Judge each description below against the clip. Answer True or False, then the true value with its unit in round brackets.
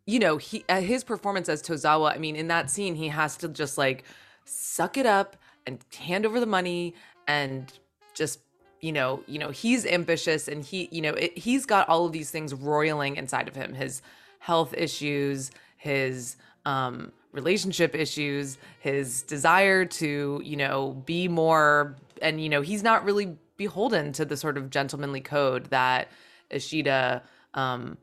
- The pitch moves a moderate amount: True (4.0 semitones)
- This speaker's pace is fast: False (165 wpm)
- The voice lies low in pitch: False (155 Hz)